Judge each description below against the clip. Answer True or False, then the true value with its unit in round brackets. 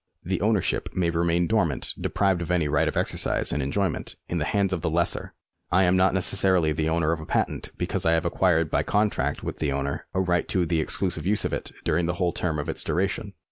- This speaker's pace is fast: True (230 wpm)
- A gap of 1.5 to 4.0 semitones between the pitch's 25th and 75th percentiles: True (2.8 semitones)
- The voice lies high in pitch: False (85 Hz)